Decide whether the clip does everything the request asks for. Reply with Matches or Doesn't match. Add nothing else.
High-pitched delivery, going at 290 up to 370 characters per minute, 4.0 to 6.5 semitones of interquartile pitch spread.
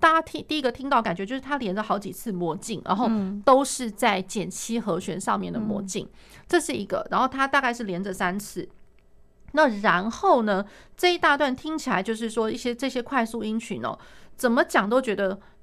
Matches